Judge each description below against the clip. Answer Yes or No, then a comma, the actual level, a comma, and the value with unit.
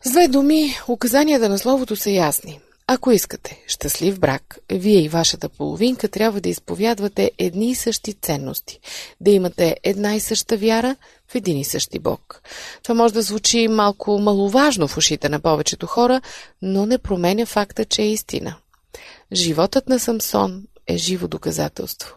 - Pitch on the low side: No, high, 210 Hz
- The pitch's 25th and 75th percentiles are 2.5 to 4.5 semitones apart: No, average, 4.9 semitones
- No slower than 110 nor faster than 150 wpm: No, average, 160 wpm